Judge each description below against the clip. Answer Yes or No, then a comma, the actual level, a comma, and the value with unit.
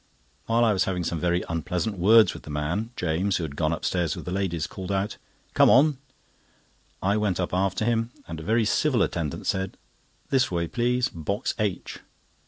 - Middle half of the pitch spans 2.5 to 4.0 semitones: No, average, 4.6 semitones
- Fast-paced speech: No, average, 190 wpm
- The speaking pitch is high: No, very low, 95 Hz